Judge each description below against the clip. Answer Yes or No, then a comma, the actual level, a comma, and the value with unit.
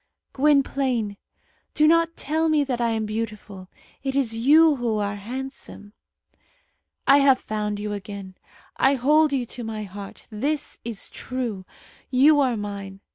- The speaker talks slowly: No, average, 145 wpm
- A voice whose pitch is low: No, high, 240 Hz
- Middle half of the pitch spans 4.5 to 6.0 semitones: Yes, average, 5.0 semitones